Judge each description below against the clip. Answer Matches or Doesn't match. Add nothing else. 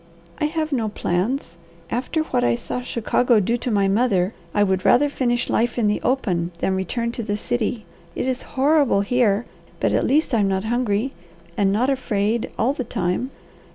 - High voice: Matches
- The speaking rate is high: Doesn't match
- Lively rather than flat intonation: Doesn't match